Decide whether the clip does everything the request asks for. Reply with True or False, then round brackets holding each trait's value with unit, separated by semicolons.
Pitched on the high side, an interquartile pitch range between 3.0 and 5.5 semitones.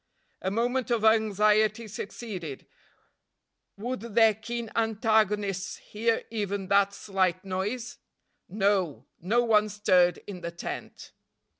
False (210 Hz; 2.6 semitones)